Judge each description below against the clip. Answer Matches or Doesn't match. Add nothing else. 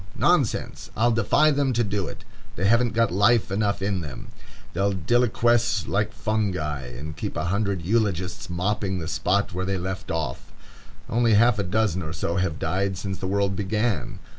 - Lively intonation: Doesn't match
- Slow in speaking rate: Doesn't match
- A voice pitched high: Doesn't match